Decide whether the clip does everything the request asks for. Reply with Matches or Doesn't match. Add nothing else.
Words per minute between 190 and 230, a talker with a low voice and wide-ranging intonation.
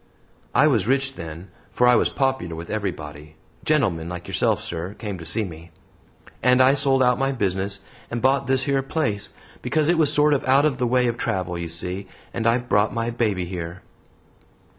Matches